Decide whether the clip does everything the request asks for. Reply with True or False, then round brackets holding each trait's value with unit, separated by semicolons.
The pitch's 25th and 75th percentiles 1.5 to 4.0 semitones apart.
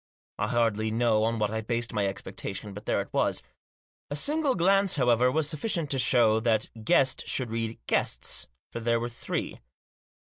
True (3.7 semitones)